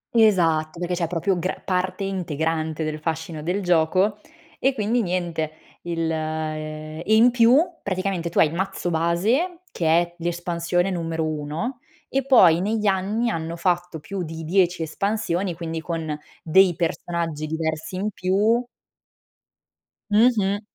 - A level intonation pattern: No, average, 3.5 semitones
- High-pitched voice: No, medium, 175 Hz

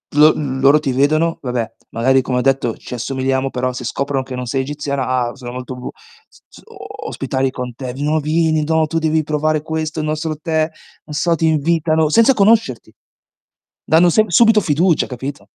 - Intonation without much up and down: No, average, 3.3 semitones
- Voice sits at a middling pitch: Yes, medium, 145 Hz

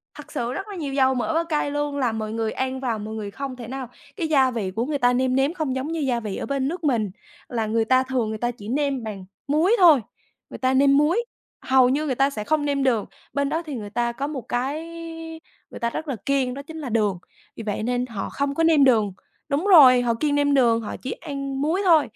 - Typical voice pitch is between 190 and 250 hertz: No, very high, 265 Hz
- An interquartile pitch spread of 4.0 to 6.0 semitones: No, average, 3.6 semitones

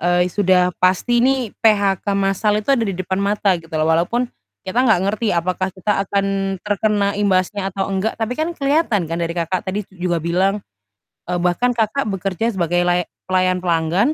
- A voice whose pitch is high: Yes, high, 195 Hz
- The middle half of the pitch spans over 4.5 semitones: No, average, 2.9 semitones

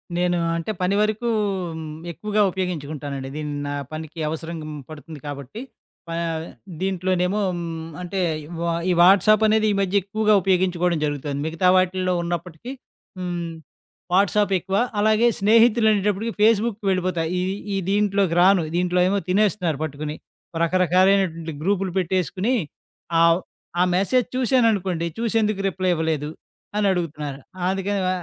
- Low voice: No, medium, 185 Hz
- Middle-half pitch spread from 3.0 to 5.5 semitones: Yes, average, 3.6 semitones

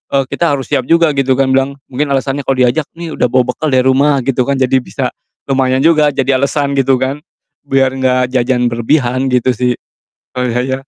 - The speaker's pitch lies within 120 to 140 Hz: Yes, low, 135 Hz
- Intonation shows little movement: Yes, narrow, 1.6 semitones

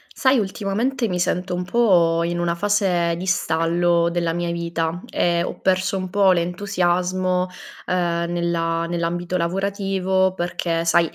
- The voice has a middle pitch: Yes, medium, 175 Hz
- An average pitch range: No, narrow, 1.9 semitones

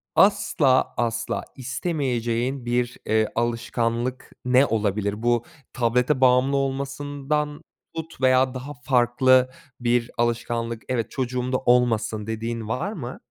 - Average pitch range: No, narrow, 2.1 semitones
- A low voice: Yes, low, 125 Hz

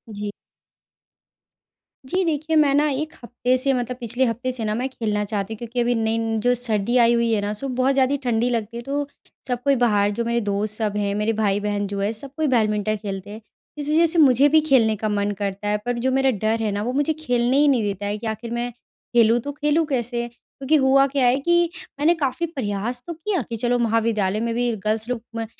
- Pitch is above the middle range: Yes, high, 235 Hz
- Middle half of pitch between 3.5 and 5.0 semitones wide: Yes, average, 3.8 semitones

